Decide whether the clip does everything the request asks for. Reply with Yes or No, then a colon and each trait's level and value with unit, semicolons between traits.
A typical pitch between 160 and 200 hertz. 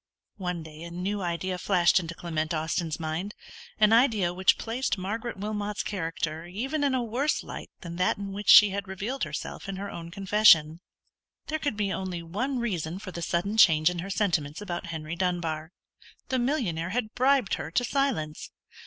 Yes: high, 190 Hz